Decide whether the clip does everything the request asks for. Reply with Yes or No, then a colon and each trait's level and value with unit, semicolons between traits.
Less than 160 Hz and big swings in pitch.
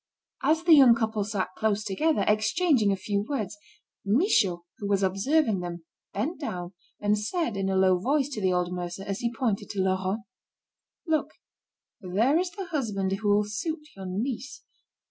No: high, 210 Hz; wide, 6.1 semitones